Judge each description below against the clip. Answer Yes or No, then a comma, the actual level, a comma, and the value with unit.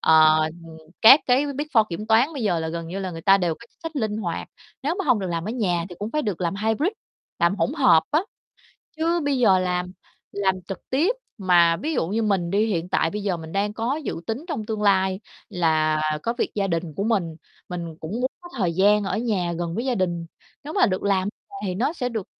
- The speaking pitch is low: No, high, 195 Hz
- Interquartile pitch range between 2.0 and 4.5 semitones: No, average, 5.1 semitones